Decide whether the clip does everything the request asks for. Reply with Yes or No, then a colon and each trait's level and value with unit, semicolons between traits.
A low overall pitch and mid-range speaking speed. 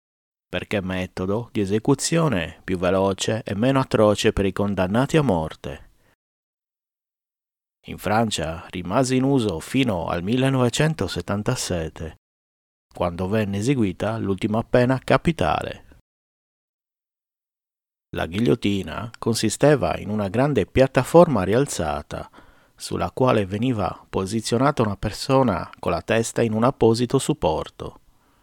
No: low, 110 Hz; slow, 105 wpm